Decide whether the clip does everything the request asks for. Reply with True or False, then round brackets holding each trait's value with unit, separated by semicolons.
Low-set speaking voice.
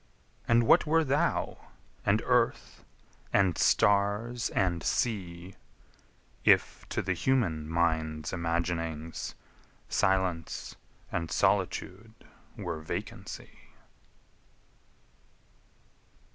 True (90 Hz)